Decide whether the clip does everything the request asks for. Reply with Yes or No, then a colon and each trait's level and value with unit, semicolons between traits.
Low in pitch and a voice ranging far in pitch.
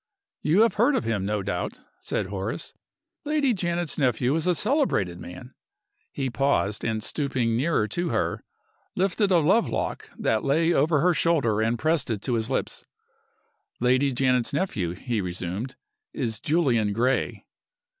Yes: low, 130 Hz; wide, 7.3 semitones